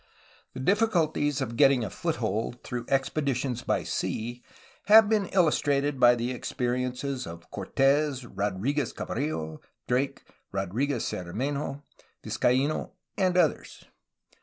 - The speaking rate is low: Yes, slow, 110 wpm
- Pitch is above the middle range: No, low, 135 Hz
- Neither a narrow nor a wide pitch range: Yes, average, 3.4 semitones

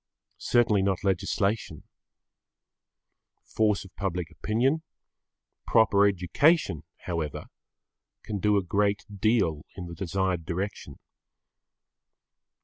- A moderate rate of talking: No, slow, 90 wpm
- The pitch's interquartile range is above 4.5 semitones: No, average, 3.3 semitones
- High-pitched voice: No, low, 100 Hz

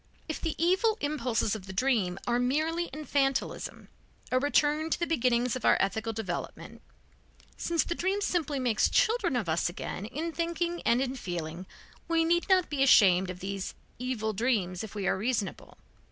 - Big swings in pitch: Yes, wide, 7.9 semitones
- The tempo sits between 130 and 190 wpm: Yes, average, 170 wpm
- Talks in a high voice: Yes, very high, 255 Hz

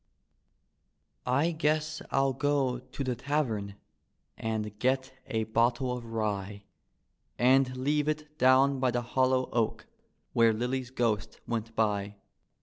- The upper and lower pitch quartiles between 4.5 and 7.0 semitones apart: No, average, 3.3 semitones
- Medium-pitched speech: No, low, 125 Hz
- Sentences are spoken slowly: Yes, slow, 125 wpm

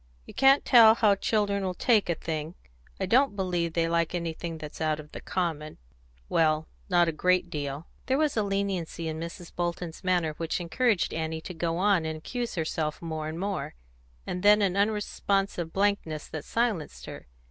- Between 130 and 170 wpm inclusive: No, average, 180 wpm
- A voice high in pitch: No, medium, 175 Hz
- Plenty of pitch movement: No, average, 3.9 semitones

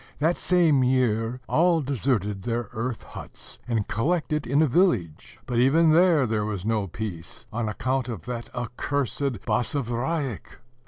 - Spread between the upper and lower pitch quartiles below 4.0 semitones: No, average, 4.7 semitones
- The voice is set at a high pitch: No, low, 125 Hz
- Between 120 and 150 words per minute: Yes, average, 145 wpm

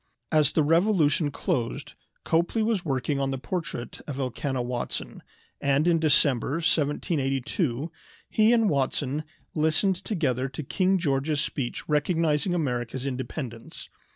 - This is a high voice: No, medium, 145 Hz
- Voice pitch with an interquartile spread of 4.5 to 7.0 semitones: No, average, 3.9 semitones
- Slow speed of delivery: Yes, slow, 125 wpm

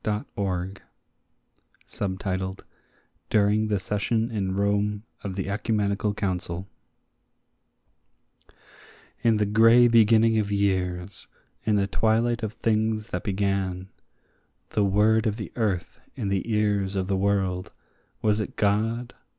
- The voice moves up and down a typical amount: No, narrow, 2.1 semitones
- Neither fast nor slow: No, slow, 120 wpm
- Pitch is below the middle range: Yes, low, 100 Hz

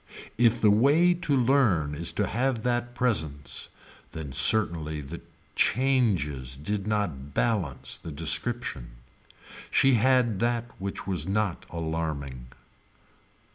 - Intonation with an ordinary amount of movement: No, wide, 7.8 semitones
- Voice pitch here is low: Yes, low, 100 Hz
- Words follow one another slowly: Yes, slow, 115 wpm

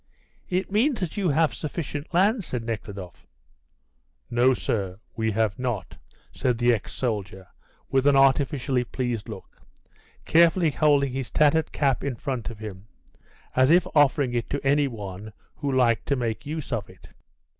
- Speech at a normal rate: Yes, average, 155 wpm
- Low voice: Yes, low, 130 Hz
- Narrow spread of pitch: No, average, 4.7 semitones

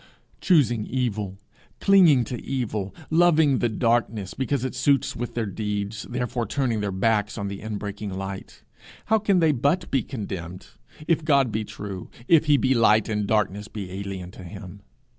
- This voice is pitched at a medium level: No, low, 110 Hz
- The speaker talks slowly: No, average, 165 wpm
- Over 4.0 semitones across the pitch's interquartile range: Yes, average, 4.9 semitones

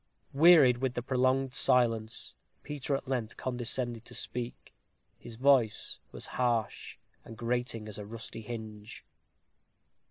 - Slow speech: Yes, slow, 125 wpm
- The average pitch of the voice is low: Yes, low, 120 Hz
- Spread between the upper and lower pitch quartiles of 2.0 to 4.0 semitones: Yes, narrow, 2.4 semitones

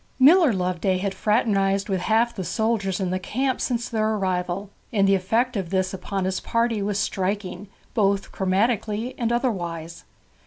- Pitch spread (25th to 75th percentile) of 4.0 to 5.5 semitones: No, average, 3.4 semitones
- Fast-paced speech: No, average, 160 wpm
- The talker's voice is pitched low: No, high, 200 Hz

